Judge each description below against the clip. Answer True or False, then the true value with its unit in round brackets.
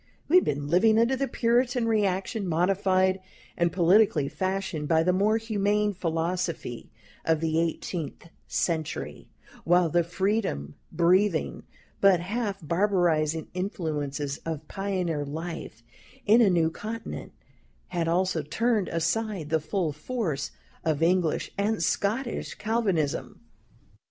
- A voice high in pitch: False (180 Hz)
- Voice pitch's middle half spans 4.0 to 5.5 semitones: True (4.3 semitones)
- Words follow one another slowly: True (120 wpm)